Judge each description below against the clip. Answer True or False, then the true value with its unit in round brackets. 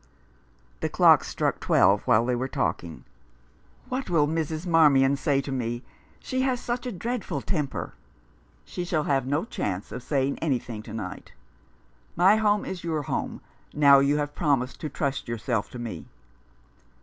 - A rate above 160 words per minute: True (170 wpm)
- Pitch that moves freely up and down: True (5.7 semitones)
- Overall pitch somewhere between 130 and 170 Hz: True (140 Hz)